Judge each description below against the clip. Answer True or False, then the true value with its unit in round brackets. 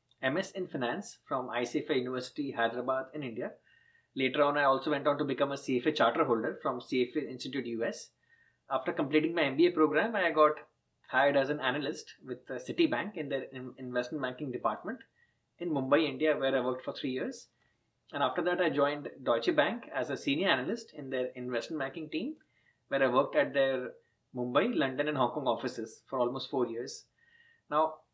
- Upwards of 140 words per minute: True (180 wpm)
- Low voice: False (145 Hz)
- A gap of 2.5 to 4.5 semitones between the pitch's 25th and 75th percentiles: True (3.5 semitones)